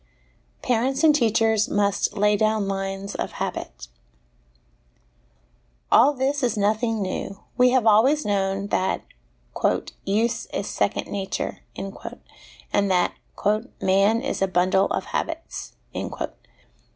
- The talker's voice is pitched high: Yes, high, 210 Hz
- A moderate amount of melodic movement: Yes, average, 3.4 semitones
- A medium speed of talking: No, slow, 115 wpm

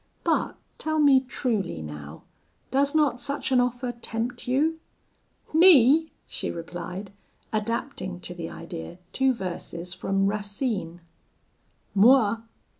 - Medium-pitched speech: No, high, 230 Hz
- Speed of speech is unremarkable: No, slow, 115 wpm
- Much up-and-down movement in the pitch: Yes, wide, 6.7 semitones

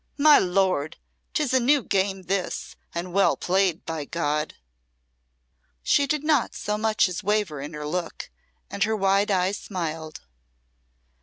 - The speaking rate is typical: Yes, average, 145 wpm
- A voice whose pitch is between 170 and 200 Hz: Yes, high, 190 Hz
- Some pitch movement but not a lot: Yes, average, 4.1 semitones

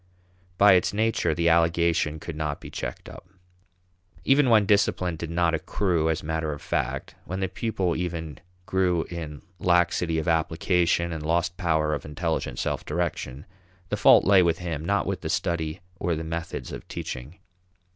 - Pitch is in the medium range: No, very low, 85 Hz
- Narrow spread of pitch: Yes, narrow, 2.0 semitones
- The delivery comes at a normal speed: Yes, average, 165 wpm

